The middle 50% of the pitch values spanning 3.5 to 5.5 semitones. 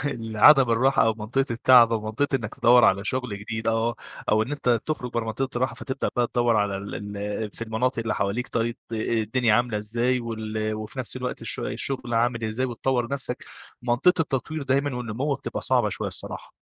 No: average, 2.8 semitones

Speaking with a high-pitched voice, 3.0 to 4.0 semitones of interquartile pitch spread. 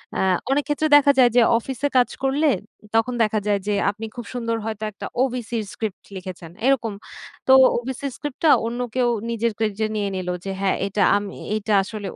Yes: high, 225 Hz; average, 3.6 semitones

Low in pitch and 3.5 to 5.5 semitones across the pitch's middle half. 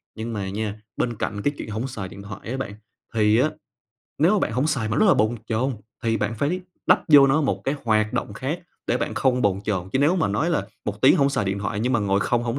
Yes: low, 115 Hz; average, 4.6 semitones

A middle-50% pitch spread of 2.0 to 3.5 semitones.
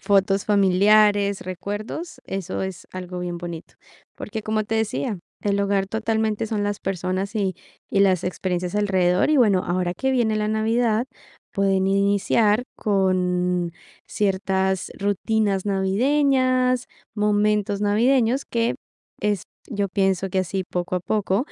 Yes: narrow, 2.5 semitones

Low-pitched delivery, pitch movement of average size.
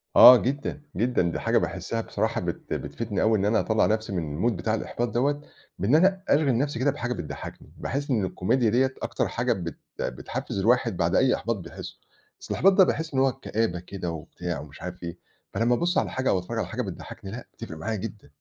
No: low, 115 Hz; wide, 6.3 semitones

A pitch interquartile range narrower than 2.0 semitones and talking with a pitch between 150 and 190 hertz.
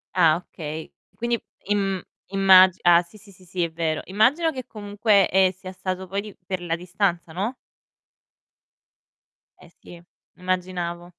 No: narrow, 2.6 semitones; medium, 185 Hz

